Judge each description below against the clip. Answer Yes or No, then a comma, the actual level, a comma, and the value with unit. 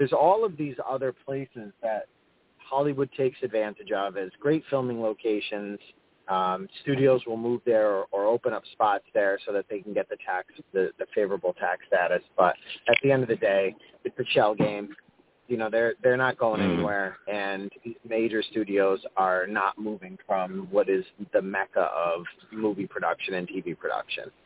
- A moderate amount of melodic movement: No, wide, 7.8 semitones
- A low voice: Yes, low, 120 Hz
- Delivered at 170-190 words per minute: Yes, average, 180 wpm